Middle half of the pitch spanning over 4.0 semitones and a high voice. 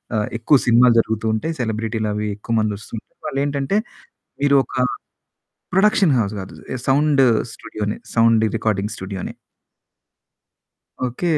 No: average, 4.5 semitones; low, 115 Hz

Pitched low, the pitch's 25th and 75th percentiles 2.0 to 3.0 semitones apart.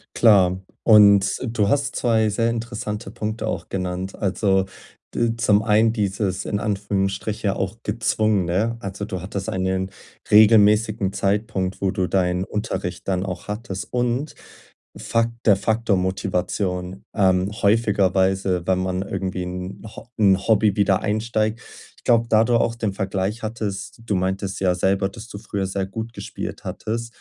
Yes: low, 100 Hz; average, 2.7 semitones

